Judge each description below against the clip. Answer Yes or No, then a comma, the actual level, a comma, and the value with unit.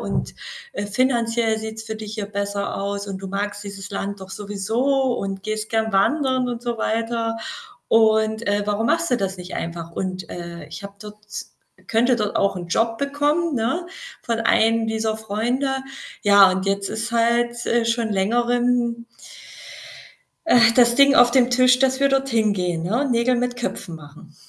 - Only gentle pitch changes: No, average, 3.2 semitones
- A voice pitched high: Yes, high, 225 Hz